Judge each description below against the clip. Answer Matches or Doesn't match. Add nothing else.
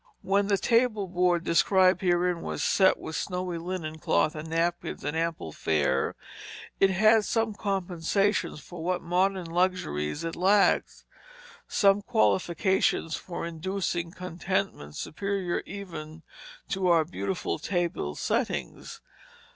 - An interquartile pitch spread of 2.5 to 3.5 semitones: Matches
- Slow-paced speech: Matches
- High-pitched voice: Doesn't match